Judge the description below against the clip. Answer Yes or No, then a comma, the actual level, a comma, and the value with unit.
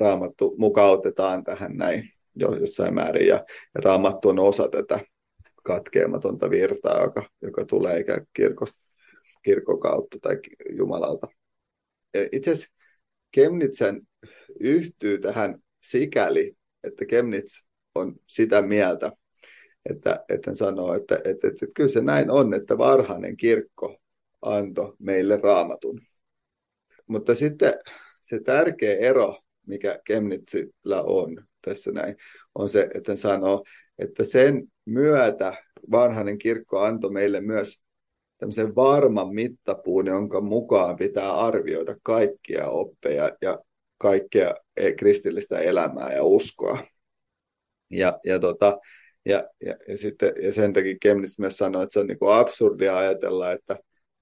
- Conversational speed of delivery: Yes, average, 120 wpm